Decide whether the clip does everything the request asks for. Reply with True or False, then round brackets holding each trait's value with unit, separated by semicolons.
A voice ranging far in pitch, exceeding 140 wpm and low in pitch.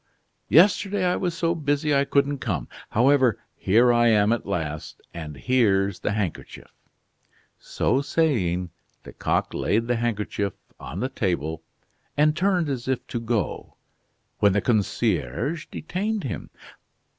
False (6.6 semitones; 135 wpm; 120 Hz)